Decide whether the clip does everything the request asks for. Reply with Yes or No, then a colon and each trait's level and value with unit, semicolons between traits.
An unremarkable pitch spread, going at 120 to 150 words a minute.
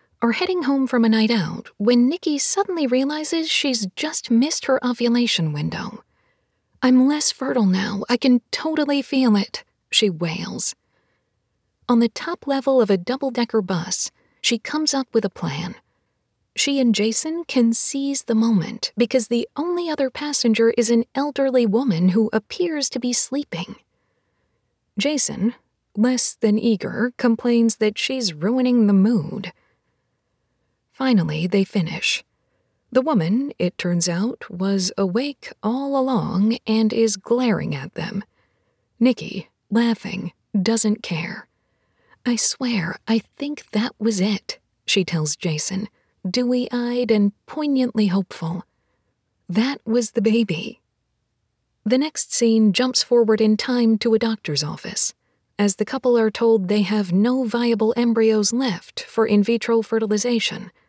Yes: average, 3.6 semitones; average, 140 wpm